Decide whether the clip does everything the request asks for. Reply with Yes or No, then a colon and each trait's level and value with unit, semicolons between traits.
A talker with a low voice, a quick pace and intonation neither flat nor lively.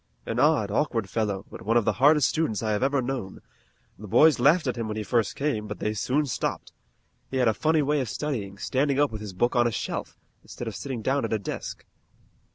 Yes: low, 120 Hz; fast, 235 wpm; average, 4.8 semitones